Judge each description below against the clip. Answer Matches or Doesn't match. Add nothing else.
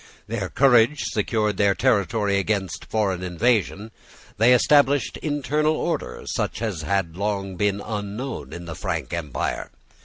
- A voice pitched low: Matches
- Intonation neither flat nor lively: Matches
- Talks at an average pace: Doesn't match